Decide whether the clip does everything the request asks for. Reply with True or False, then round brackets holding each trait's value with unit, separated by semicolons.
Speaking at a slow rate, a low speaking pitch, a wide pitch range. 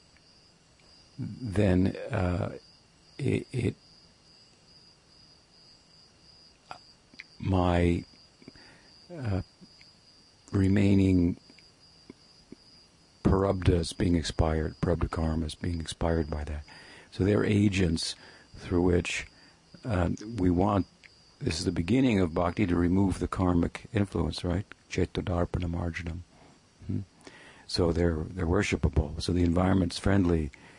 False (90 wpm; 90 Hz; 2.6 semitones)